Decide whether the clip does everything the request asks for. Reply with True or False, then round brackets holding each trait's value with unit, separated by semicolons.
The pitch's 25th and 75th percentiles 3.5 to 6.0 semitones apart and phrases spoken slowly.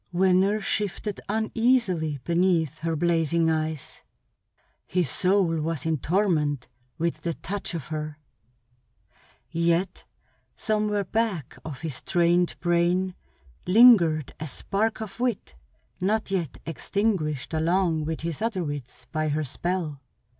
True (3.9 semitones; 120 wpm)